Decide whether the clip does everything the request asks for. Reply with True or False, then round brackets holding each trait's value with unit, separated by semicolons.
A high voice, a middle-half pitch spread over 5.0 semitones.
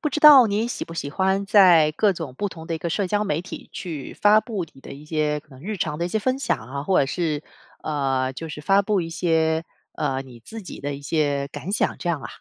False (165 Hz; 5.4 semitones)